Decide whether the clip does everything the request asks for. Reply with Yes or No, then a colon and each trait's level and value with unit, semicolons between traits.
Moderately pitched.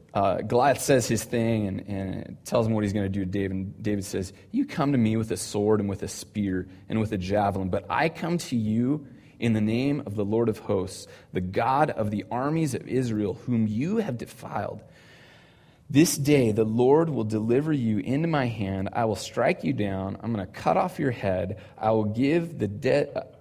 No: low, 110 Hz